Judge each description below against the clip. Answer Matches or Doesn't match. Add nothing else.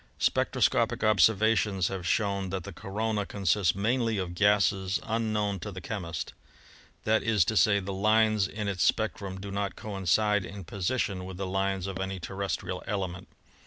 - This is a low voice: Matches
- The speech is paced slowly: Doesn't match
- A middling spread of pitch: Doesn't match